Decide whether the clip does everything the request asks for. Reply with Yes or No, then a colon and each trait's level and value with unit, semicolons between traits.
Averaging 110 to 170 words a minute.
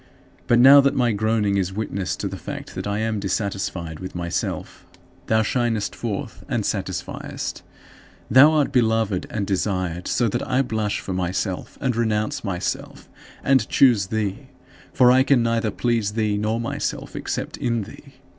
Yes: average, 160 wpm